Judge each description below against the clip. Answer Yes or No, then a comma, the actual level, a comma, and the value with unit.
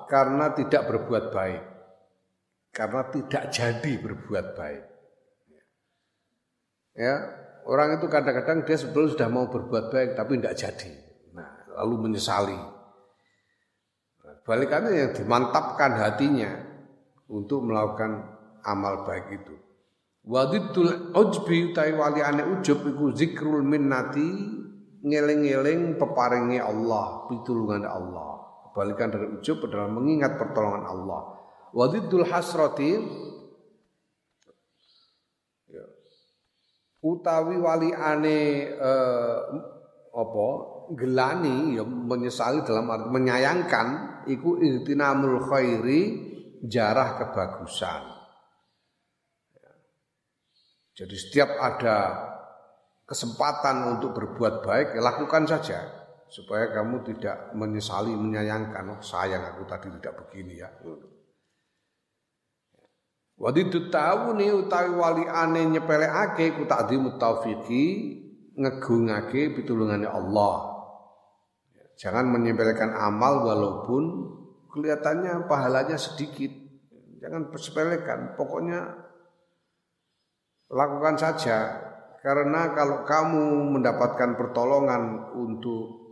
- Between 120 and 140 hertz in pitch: Yes, low, 135 Hz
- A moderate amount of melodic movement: No, wide, 5.7 semitones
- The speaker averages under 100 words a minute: Yes, slow, 85 wpm